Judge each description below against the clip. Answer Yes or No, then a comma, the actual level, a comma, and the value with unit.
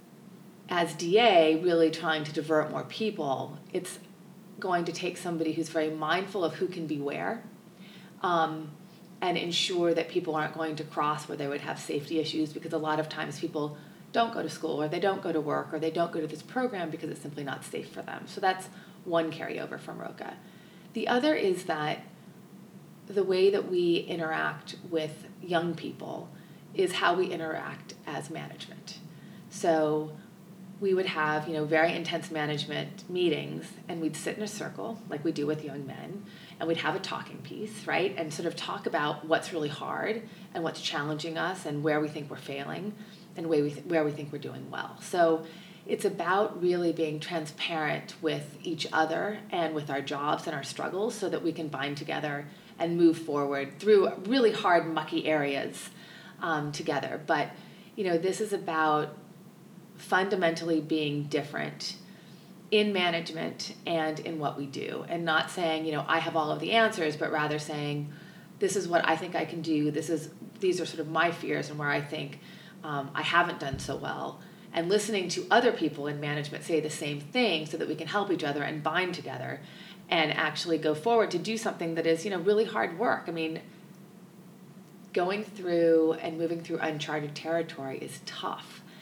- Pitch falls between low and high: Yes, medium, 165 Hz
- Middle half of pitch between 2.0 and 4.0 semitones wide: Yes, average, 3.3 semitones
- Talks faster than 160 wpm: Yes, average, 190 wpm